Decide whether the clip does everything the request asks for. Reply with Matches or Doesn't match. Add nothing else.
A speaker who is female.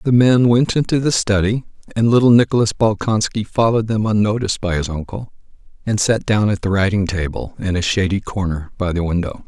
Doesn't match